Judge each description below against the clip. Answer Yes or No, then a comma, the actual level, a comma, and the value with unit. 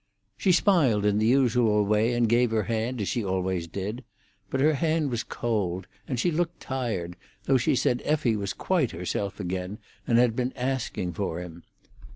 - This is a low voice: Yes, low, 115 Hz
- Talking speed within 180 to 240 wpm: Yes, average, 185 wpm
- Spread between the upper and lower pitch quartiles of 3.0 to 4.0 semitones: No, average, 4.7 semitones